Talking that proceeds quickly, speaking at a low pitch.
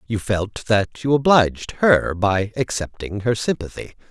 No: average, 145 wpm; low, 110 Hz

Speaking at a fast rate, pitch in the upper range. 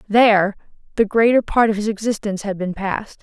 No: average, 185 wpm; high, 210 Hz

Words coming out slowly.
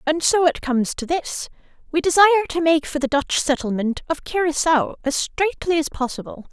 No: average, 185 wpm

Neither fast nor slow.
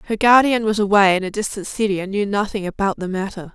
No: fast, 235 wpm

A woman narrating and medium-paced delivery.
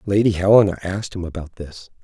No: male; average, 175 wpm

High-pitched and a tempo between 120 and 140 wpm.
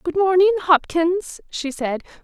Yes: very high, 340 Hz; slow, 135 wpm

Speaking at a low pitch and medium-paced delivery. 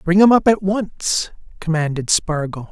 No: medium, 175 Hz; average, 155 wpm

